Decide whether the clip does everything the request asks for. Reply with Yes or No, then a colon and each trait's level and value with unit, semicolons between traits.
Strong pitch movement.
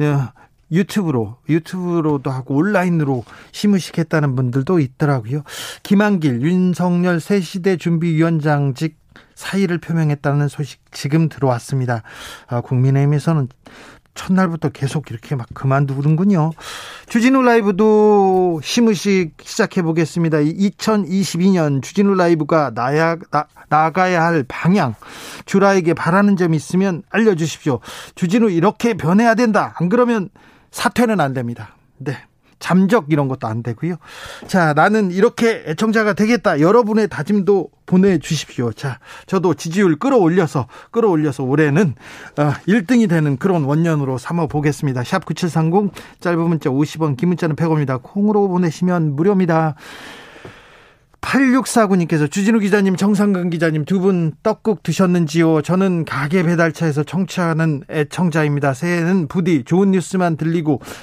No: average, 4.6 semitones